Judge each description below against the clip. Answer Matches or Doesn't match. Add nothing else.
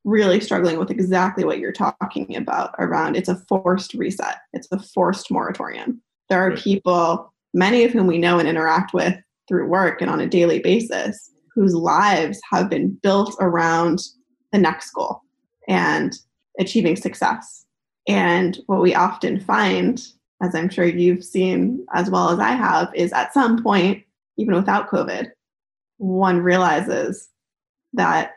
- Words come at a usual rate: Matches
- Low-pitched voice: Doesn't match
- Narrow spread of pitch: Matches